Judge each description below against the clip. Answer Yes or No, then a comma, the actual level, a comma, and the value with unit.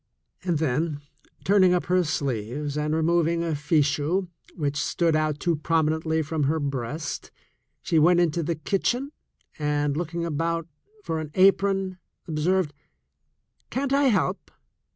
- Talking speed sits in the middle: No, slow, 130 wpm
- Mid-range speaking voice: Yes, medium, 160 Hz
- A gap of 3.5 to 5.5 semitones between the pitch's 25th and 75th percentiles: No, average, 3.0 semitones